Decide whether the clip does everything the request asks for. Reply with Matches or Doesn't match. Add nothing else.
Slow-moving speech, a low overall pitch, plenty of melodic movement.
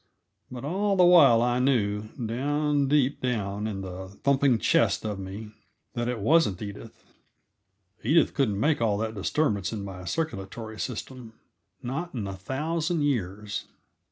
Doesn't match